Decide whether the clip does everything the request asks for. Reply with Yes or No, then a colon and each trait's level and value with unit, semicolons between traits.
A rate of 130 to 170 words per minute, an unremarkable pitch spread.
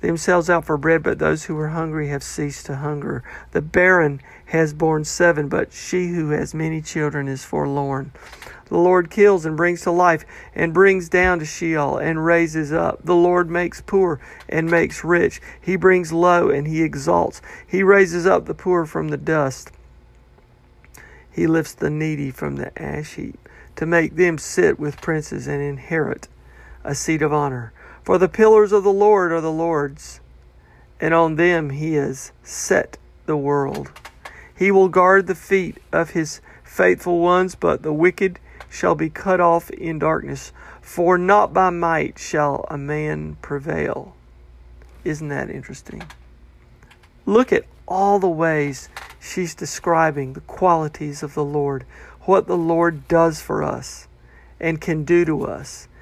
Yes: average, 160 wpm; average, 3.7 semitones